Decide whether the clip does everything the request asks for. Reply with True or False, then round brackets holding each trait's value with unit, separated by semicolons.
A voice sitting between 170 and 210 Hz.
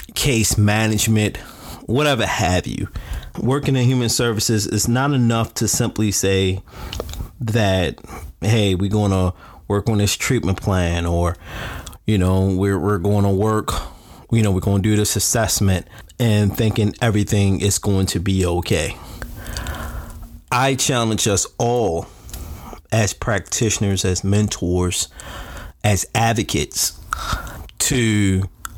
False (100 Hz)